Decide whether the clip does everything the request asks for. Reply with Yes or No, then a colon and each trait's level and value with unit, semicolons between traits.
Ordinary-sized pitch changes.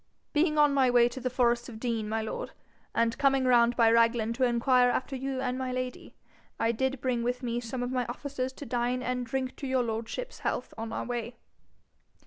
No: narrow, 1.8 semitones